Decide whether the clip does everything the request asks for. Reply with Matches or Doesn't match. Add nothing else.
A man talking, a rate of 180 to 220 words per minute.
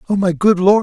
Doesn't match